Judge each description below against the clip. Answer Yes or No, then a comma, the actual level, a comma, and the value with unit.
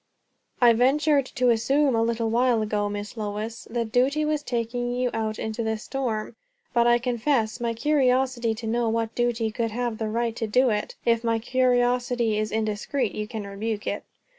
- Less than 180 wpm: No, average, 185 wpm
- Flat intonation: Yes, narrow, 2.1 semitones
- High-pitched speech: Yes, high, 235 Hz